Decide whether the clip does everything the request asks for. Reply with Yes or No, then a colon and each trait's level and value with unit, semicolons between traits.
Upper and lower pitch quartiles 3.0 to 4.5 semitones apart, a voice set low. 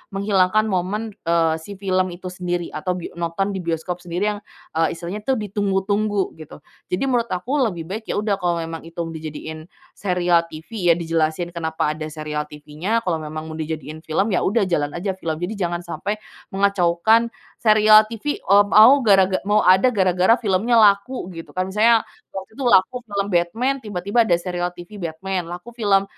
No: average, 3.6 semitones; medium, 185 Hz